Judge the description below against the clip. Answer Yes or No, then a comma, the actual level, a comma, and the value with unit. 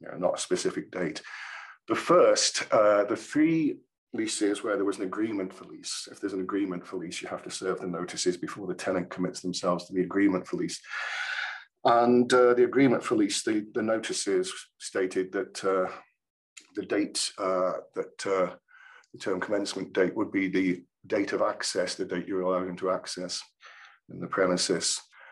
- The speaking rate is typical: Yes, average, 185 wpm